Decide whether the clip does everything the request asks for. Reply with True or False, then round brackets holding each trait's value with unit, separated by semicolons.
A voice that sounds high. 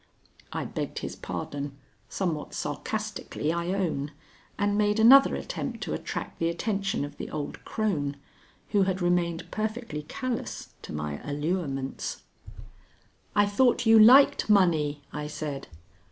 False (175 Hz)